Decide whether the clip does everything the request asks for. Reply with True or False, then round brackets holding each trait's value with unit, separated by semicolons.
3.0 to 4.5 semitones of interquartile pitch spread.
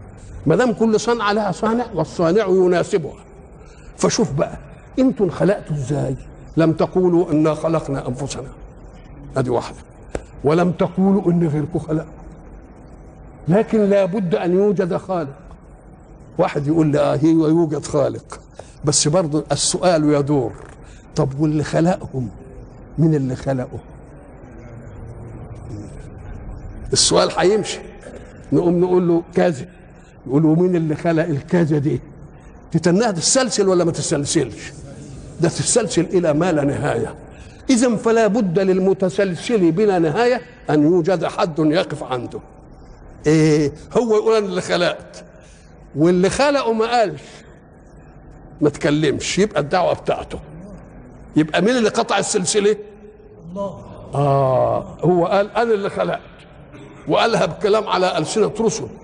False (4.9 semitones)